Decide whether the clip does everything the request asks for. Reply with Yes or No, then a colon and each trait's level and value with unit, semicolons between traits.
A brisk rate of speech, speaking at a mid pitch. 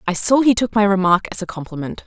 No: fast, 260 wpm; high, 200 Hz